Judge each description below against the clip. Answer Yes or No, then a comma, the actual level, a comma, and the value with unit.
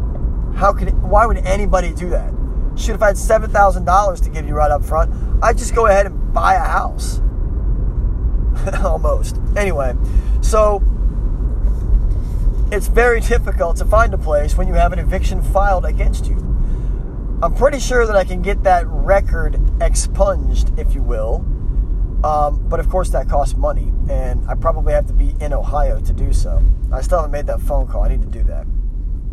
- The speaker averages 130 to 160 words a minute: No, average, 180 wpm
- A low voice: Yes, very low, 90 Hz